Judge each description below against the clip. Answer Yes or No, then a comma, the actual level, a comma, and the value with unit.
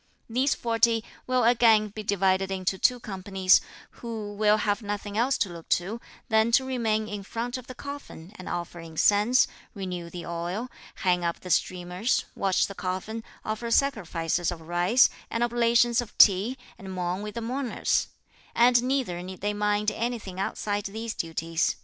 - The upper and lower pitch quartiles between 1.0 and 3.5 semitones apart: No, average, 4.2 semitones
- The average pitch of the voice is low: No, high, 210 Hz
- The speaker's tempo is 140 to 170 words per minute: Yes, average, 165 wpm